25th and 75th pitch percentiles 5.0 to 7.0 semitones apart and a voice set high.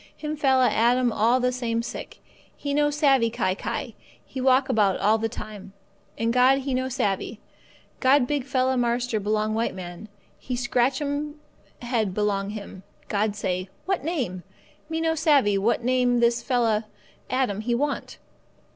No: average, 3.7 semitones; high, 245 Hz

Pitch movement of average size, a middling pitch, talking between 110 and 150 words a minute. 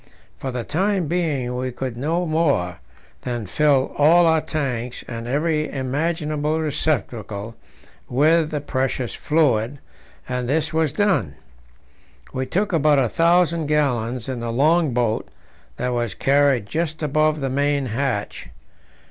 Yes: average, 4.1 semitones; medium, 145 Hz; slow, 135 wpm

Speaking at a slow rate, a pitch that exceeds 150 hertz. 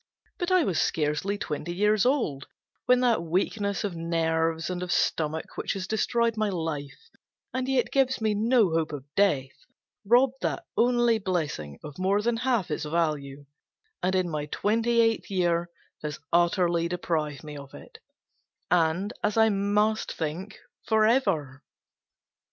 No: average, 150 wpm; medium, 185 Hz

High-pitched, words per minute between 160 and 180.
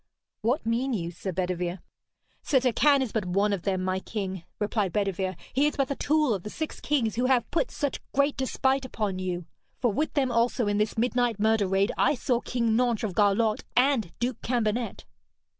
No: high, 225 Hz; average, 195 wpm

